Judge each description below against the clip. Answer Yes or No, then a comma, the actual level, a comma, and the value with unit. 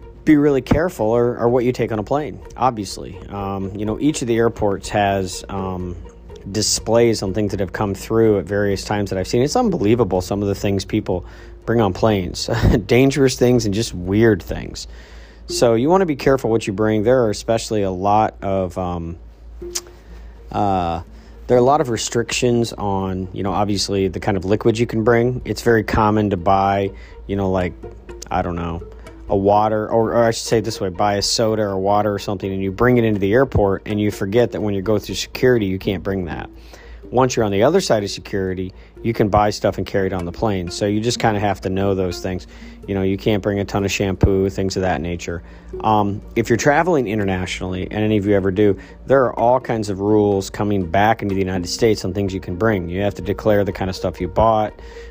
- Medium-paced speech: No, fast, 230 wpm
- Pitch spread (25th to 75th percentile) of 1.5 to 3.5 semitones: Yes, average, 3.0 semitones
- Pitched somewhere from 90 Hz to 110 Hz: Yes, low, 100 Hz